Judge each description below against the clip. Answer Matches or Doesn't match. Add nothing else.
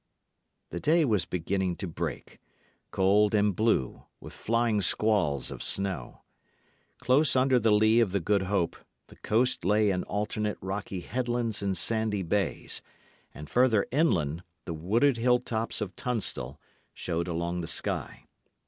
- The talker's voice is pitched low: Matches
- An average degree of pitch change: Matches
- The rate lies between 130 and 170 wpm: Matches